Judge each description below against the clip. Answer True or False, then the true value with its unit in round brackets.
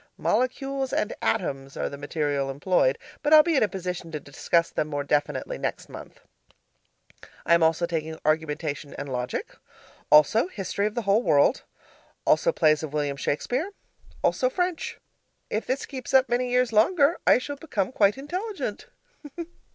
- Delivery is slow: False (160 wpm)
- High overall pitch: True (195 Hz)